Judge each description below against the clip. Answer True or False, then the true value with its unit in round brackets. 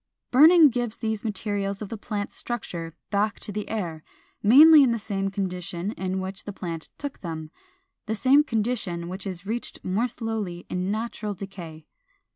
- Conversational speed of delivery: True (165 wpm)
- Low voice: False (205 Hz)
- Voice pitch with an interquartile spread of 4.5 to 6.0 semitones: False (3.7 semitones)